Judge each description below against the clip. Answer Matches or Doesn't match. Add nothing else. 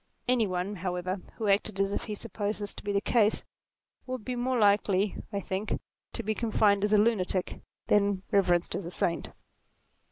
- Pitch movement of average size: Doesn't match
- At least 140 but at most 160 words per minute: Doesn't match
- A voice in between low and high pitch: Doesn't match